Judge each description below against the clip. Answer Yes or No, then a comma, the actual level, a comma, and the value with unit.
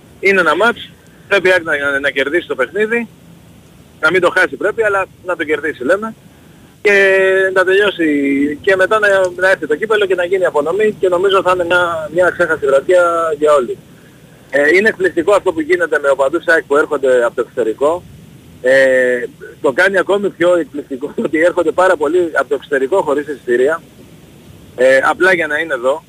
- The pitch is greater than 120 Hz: Yes, medium, 185 Hz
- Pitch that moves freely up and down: Yes, wide, 5.7 semitones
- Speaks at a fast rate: Yes, fast, 180 wpm